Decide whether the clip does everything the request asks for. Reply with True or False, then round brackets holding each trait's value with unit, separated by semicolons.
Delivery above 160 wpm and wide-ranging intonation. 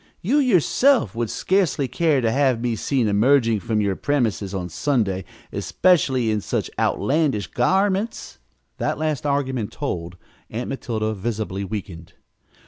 False (135 wpm; 5.8 semitones)